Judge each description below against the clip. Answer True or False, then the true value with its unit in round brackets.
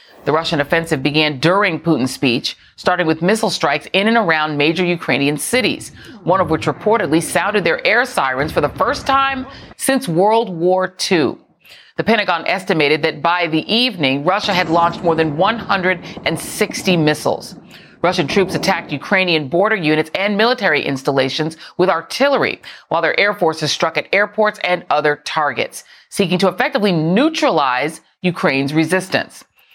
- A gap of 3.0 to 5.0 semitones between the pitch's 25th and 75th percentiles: True (4.6 semitones)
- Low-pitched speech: False (175 Hz)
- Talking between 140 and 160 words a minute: True (150 wpm)